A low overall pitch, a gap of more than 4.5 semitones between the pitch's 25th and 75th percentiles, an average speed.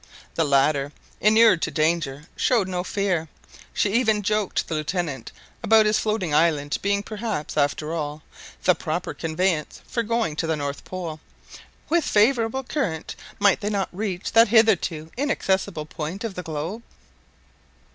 No: medium, 185 Hz; wide, 5.6 semitones; average, 150 wpm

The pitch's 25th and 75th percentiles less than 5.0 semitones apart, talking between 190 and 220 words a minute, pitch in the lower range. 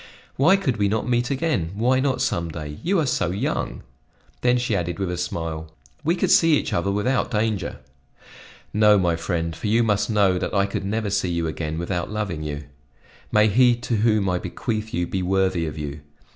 No: average, 5.3 semitones; average, 200 wpm; low, 100 Hz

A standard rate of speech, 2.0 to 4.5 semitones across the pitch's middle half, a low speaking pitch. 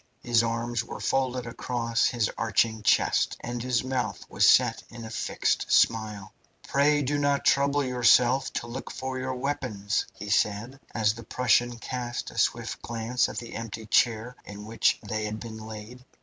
Yes: average, 170 wpm; narrow, 2.5 semitones; low, 120 Hz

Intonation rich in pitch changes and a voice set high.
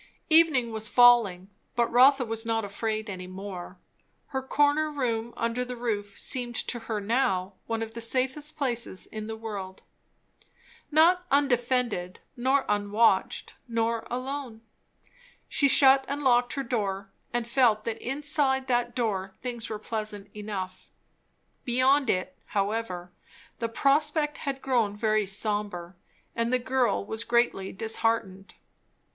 No: average, 3.9 semitones; high, 230 Hz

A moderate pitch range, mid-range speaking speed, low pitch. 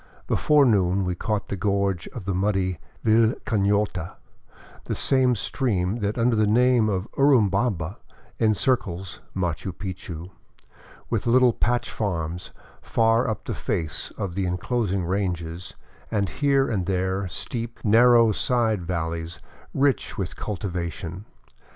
No: average, 4.2 semitones; slow, 125 wpm; low, 100 Hz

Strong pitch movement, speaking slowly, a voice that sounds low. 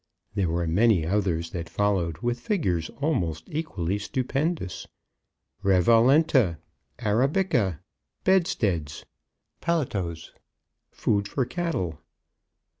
Yes: wide, 8.1 semitones; slow, 85 wpm; low, 100 Hz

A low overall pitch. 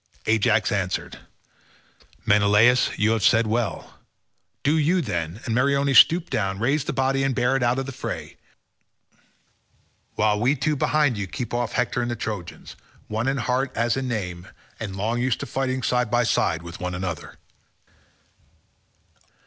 Yes: low, 120 Hz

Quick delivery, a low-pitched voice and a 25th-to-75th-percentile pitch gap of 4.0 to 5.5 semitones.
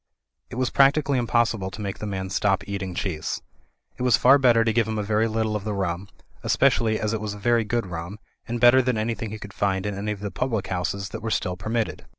No: fast, 245 wpm; low, 110 Hz; average, 3.1 semitones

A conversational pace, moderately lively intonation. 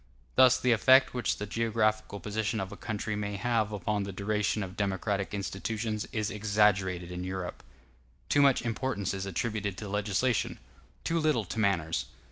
No: average, 160 wpm; narrow, 2.3 semitones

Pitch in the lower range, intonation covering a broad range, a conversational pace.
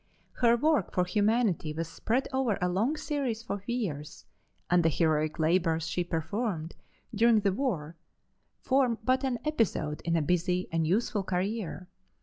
No: high, 190 Hz; wide, 6.2 semitones; average, 150 wpm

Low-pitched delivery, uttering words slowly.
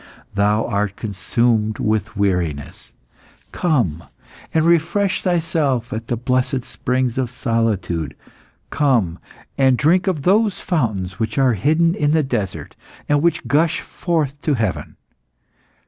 Yes: low, 125 Hz; slow, 125 wpm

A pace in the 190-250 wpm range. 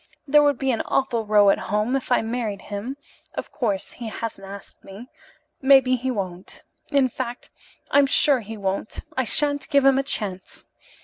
No: average, 180 wpm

